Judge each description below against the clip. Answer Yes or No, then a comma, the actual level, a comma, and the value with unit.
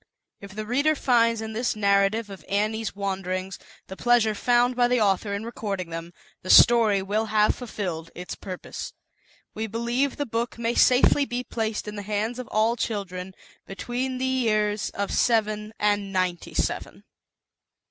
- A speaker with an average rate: Yes, average, 160 wpm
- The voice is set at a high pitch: Yes, high, 215 Hz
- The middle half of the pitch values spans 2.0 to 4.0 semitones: Yes, average, 3.1 semitones